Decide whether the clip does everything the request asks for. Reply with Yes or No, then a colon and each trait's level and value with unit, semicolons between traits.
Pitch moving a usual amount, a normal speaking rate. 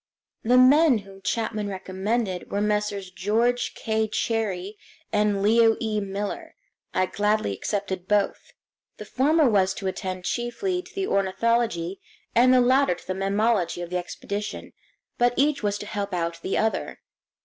Yes: average, 3.6 semitones; average, 150 wpm